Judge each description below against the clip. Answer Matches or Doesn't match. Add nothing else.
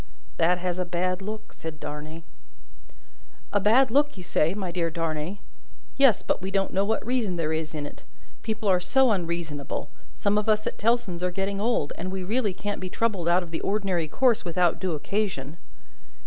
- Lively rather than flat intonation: Doesn't match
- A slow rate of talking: Doesn't match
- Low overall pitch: Doesn't match